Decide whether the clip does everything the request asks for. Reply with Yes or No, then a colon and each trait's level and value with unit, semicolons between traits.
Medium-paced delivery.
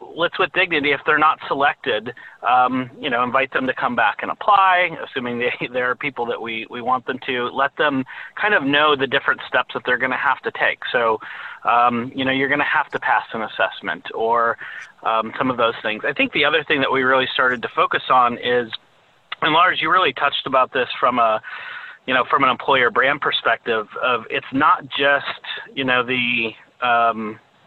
No: fast, 215 wpm